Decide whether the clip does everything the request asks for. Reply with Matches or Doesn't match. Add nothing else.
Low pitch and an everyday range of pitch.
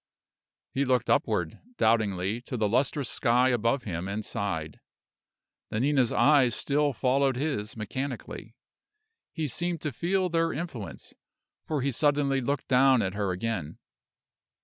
Matches